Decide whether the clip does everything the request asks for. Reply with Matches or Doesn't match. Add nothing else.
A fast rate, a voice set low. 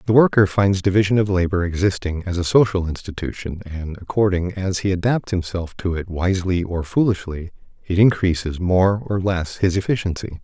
Doesn't match